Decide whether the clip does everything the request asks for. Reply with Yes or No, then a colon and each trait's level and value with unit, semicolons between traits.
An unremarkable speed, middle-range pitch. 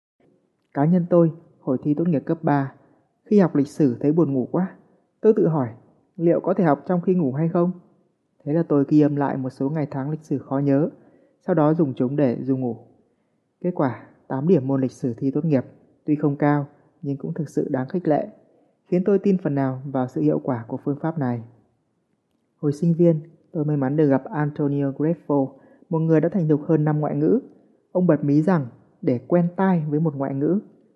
Yes: average, 220 wpm; medium, 150 Hz